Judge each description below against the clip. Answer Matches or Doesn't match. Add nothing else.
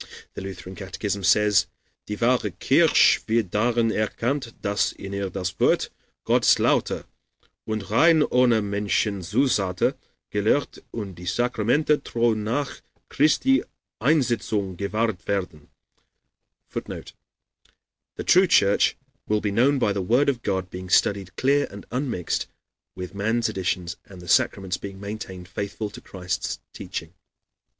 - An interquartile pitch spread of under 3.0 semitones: Doesn't match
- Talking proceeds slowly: Matches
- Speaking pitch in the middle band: Doesn't match